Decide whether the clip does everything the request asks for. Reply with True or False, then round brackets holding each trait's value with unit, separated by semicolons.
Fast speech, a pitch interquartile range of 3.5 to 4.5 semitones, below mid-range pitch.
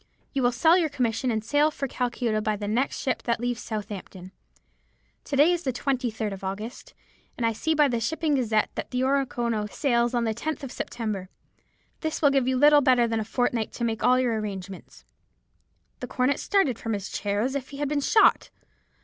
False (210 wpm; 4.1 semitones; 245 Hz)